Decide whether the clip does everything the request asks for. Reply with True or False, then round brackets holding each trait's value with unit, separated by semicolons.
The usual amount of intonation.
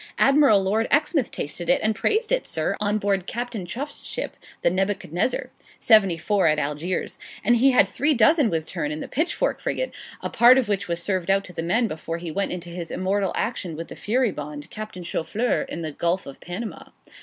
False (5.7 semitones)